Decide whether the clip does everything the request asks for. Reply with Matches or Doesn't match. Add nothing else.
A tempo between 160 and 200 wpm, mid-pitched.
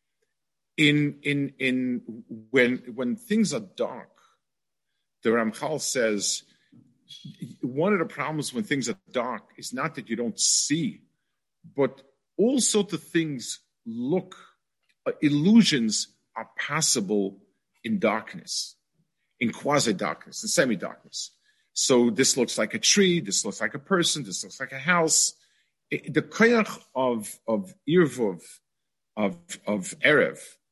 Doesn't match